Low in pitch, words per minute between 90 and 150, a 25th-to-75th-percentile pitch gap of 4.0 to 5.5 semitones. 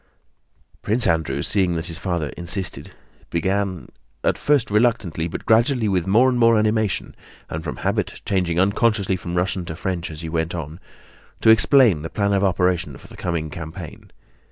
No: very low, 90 Hz; average, 160 wpm; average, 4.4 semitones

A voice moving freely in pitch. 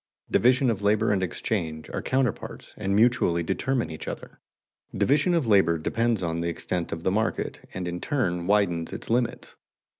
Yes: wide, 5.7 semitones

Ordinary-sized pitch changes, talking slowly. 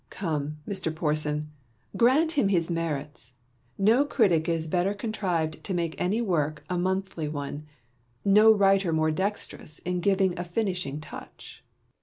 No: average, 4.2 semitones; average, 145 wpm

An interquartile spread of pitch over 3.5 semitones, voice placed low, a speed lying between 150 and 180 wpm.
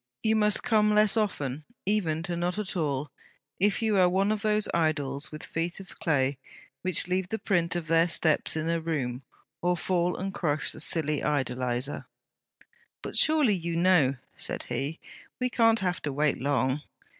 No: average, 5.0 semitones; medium, 170 Hz; average, 175 wpm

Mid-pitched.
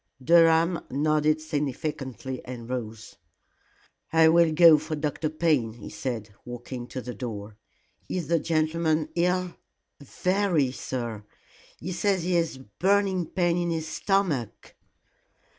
Yes: medium, 155 Hz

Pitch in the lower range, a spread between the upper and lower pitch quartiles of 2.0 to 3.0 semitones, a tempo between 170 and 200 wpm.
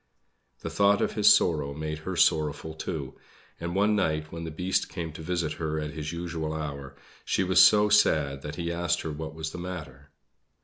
Yes: very low, 80 Hz; narrow, 2.4 semitones; average, 195 wpm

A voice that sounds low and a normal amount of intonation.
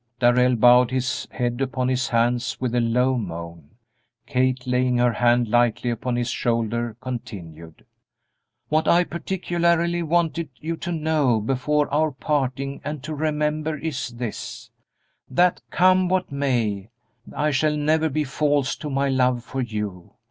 Yes: low, 130 Hz; average, 4.1 semitones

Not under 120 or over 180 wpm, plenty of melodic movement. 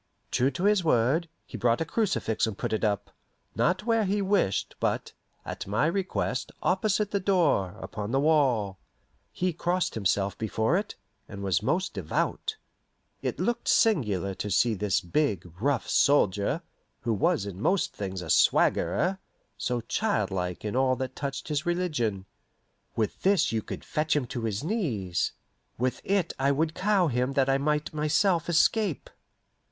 Yes: average, 160 wpm; wide, 9.0 semitones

